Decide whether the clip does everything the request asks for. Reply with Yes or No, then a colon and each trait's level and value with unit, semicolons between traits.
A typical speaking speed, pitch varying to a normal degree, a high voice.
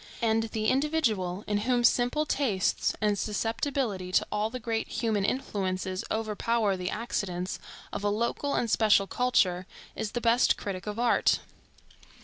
Yes: average, 145 wpm; average, 3.3 semitones; high, 220 Hz